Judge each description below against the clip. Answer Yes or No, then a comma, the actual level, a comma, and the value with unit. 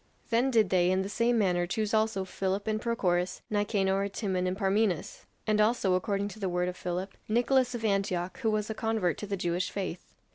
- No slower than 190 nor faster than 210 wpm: Yes, fast, 205 wpm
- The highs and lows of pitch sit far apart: No, average, 3.1 semitones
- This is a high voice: Yes, high, 200 Hz